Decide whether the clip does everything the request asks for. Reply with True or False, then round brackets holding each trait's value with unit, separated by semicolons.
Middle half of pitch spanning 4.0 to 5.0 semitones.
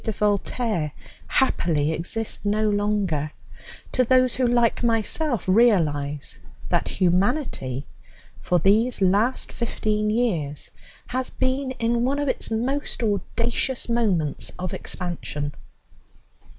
False (5.4 semitones)